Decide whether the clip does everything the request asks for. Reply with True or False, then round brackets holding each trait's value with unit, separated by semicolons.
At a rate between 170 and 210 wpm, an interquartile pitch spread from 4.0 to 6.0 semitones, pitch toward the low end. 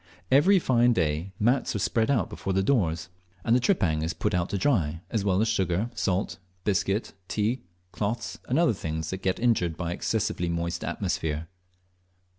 True (175 wpm; 5.2 semitones; 95 Hz)